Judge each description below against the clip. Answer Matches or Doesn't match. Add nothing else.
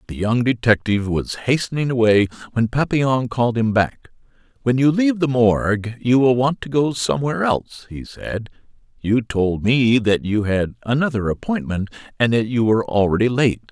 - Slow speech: Doesn't match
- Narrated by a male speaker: Matches